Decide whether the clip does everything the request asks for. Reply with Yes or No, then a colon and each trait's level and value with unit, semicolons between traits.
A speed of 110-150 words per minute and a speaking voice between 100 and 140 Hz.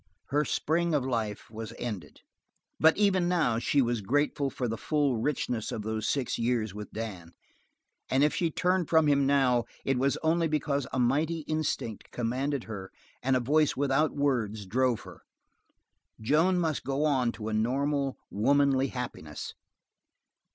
No: average, 160 wpm; low, 135 Hz